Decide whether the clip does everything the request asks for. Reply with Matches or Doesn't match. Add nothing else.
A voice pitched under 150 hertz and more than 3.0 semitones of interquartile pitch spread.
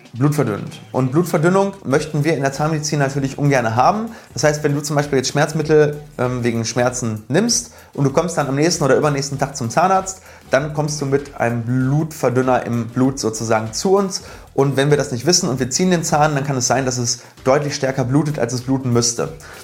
Matches